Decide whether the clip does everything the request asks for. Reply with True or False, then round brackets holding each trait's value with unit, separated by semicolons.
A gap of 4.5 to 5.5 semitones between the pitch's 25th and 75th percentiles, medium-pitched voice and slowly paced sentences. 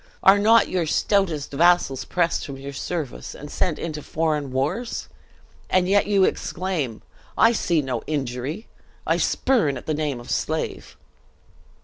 False (5.2 semitones; 155 Hz; 145 wpm)